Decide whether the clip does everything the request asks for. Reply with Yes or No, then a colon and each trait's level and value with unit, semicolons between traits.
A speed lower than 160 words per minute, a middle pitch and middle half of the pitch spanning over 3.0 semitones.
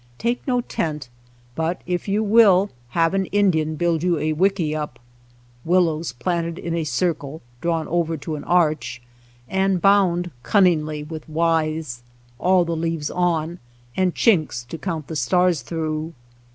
No: average, 145 wpm; medium, 165 Hz; average, 2.7 semitones